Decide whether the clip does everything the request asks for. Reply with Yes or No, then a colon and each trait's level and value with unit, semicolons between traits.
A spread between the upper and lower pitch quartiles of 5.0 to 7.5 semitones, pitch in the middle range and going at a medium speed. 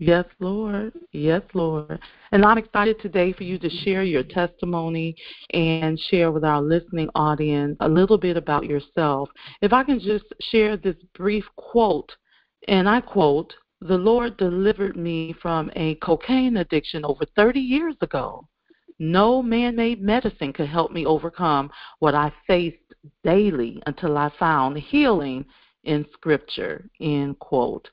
Yes: average, 5.3 semitones; medium, 175 Hz; average, 145 wpm